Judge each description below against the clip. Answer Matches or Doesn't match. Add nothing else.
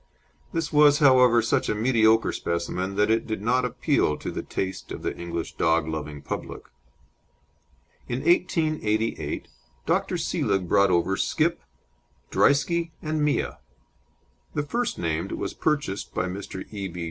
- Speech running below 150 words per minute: Matches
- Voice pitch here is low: Matches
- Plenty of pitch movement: Matches